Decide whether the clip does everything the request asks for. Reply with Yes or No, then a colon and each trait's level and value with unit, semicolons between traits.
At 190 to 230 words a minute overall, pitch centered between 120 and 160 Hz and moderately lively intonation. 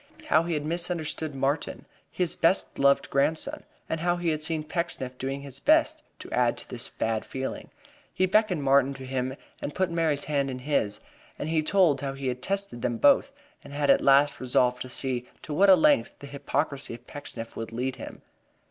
Yes: average, 200 wpm; medium, 140 Hz; average, 3.8 semitones